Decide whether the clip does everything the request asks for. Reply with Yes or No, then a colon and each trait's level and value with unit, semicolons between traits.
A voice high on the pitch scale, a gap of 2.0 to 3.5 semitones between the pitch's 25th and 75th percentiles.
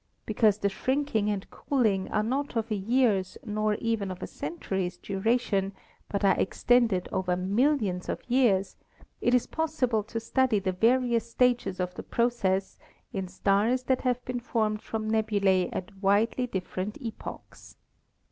No: high, 215 Hz; average, 4.0 semitones